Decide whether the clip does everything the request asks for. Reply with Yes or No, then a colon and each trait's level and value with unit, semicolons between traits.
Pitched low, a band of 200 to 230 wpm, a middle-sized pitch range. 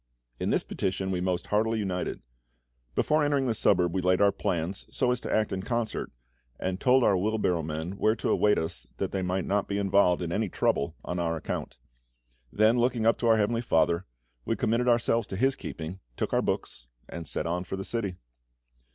Yes: low, 100 Hz; fast, 205 wpm; average, 4.1 semitones